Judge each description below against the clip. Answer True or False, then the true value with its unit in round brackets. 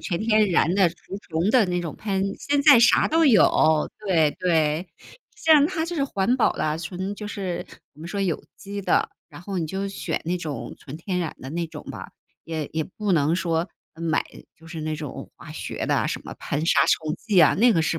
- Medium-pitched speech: True (180 Hz)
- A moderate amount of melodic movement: True (4.2 semitones)